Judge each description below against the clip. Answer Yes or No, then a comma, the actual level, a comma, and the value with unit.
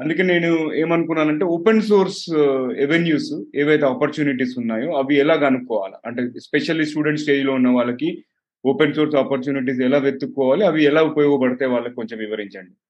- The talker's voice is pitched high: No, medium, 140 Hz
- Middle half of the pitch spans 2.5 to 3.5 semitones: Yes, average, 3.0 semitones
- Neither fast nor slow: No, fast, 140 wpm